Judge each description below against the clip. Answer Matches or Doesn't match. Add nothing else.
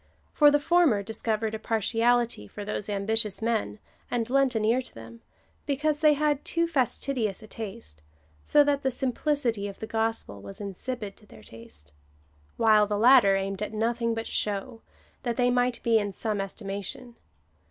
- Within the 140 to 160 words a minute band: Doesn't match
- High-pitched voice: Matches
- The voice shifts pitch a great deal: Doesn't match